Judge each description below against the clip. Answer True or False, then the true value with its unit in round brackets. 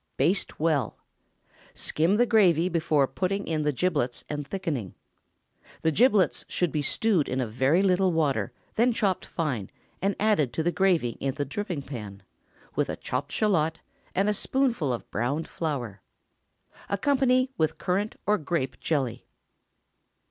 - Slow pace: False (150 wpm)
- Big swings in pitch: True (6.1 semitones)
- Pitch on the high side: False (160 Hz)